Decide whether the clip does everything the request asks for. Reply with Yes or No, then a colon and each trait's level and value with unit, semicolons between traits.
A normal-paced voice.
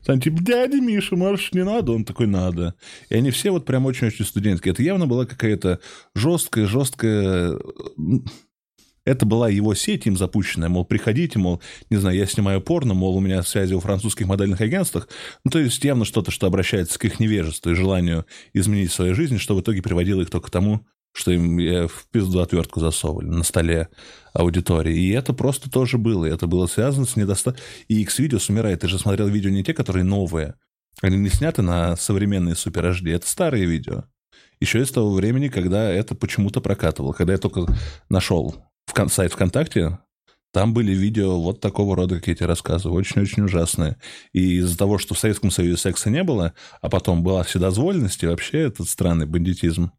No: fast, 180 wpm